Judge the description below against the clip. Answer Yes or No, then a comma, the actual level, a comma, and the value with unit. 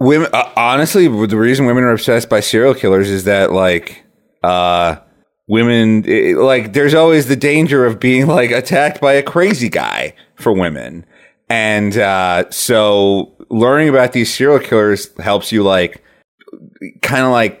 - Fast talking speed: No, average, 155 wpm